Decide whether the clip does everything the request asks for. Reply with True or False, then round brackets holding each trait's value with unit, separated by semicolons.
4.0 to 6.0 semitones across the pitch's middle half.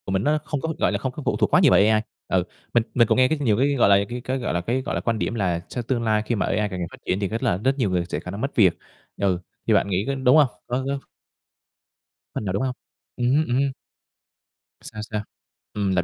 True (4.9 semitones)